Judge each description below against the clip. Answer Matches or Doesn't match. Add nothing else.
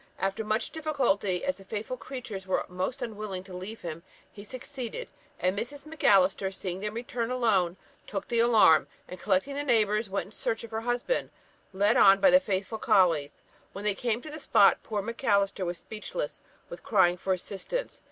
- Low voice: Doesn't match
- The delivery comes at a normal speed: Matches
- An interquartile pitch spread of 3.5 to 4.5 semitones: Matches